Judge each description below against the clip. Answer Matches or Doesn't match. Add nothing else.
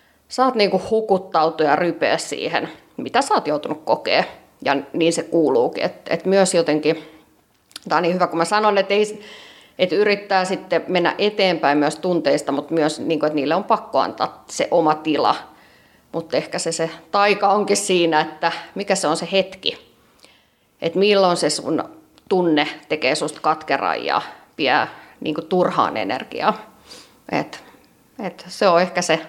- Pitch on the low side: Doesn't match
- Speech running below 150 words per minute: Doesn't match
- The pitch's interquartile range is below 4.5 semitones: Matches